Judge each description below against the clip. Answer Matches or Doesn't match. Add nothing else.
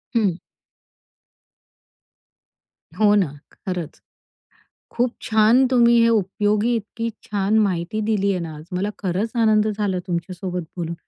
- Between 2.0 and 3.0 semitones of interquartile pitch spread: Doesn't match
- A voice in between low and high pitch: Doesn't match